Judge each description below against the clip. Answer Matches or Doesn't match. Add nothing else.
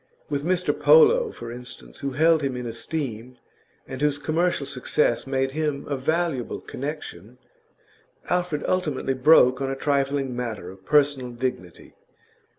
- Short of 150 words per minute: Matches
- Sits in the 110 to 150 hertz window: Matches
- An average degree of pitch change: Matches